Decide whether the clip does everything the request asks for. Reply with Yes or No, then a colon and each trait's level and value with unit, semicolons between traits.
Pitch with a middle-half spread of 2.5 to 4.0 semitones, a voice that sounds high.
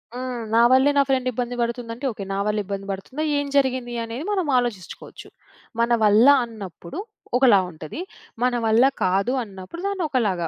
No: average, 4.4 semitones; high, 235 Hz